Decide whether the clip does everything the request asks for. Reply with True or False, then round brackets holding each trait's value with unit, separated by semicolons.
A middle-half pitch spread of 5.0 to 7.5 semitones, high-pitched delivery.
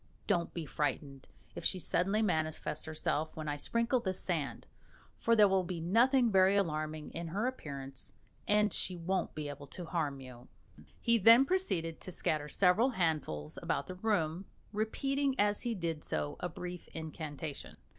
False (5.3 semitones; 175 Hz)